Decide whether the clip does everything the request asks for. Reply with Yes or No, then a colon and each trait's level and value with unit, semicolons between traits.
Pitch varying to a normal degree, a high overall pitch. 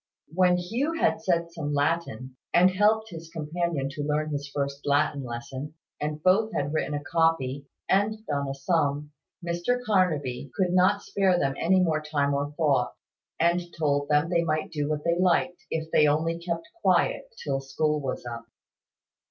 No: average, 3.7 semitones; medium, 155 Hz